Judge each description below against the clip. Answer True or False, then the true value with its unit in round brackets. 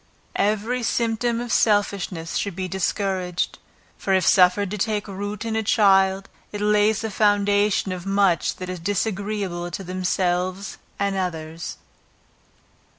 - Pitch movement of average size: False (2.3 semitones)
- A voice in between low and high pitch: False (195 Hz)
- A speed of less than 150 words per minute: True (135 wpm)